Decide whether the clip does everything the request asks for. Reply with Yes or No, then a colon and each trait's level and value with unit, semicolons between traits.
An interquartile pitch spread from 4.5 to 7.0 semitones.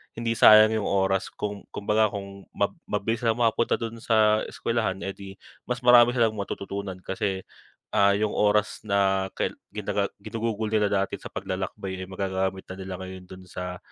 No: narrow, 2.4 semitones